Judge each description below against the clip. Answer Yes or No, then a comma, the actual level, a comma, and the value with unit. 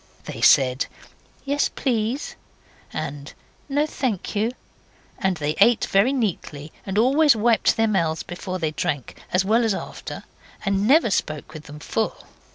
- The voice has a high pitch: Yes, high, 200 Hz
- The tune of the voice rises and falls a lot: Yes, wide, 7.1 semitones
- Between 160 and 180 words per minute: No, average, 150 wpm